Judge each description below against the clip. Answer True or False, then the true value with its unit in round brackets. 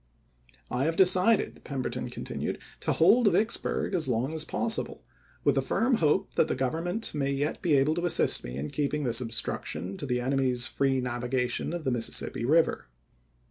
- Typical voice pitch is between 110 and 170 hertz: True (140 Hz)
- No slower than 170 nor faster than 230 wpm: True (185 wpm)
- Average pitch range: False (5.7 semitones)